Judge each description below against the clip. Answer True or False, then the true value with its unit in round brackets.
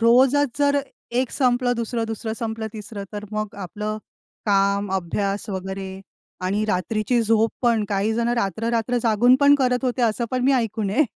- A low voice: False (225 Hz)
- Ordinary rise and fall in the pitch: True (3.2 semitones)